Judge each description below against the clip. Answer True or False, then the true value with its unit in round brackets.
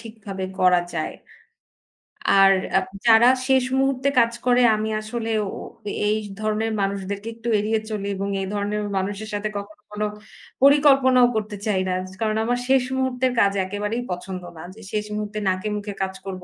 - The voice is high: True (215 Hz)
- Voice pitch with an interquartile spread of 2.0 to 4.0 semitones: True (2.9 semitones)